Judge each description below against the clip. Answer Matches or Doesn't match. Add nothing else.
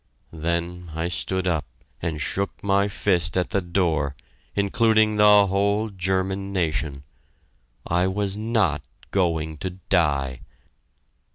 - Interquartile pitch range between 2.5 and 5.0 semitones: Matches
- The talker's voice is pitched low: Matches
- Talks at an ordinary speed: Doesn't match